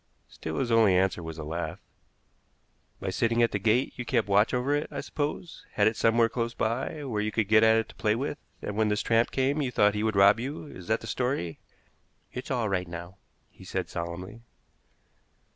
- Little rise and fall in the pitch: No, average, 3.8 semitones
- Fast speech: Yes, fast, 210 wpm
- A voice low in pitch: Yes, low, 110 Hz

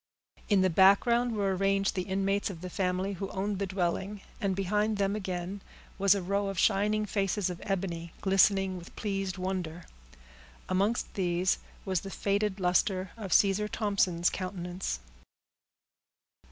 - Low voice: No, high, 195 Hz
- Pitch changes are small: Yes, narrow, 1.6 semitones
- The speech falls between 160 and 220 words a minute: No, average, 145 wpm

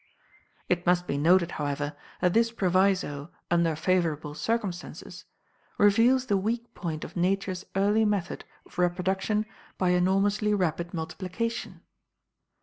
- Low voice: No, medium, 185 Hz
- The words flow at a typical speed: No, slow, 120 wpm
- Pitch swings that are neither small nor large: Yes, average, 3.2 semitones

